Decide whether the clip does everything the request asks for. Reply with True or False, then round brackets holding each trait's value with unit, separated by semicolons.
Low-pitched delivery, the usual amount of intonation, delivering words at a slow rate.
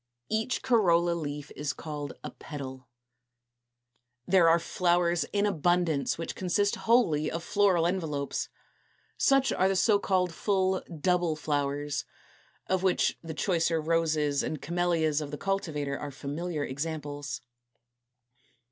False (165 Hz; 3.9 semitones; 130 wpm)